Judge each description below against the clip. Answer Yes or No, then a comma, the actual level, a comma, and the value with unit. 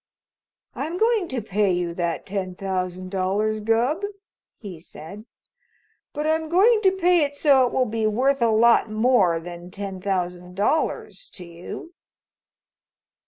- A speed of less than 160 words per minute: Yes, average, 145 wpm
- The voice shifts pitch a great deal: Yes, wide, 7.5 semitones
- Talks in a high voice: Yes, high, 215 Hz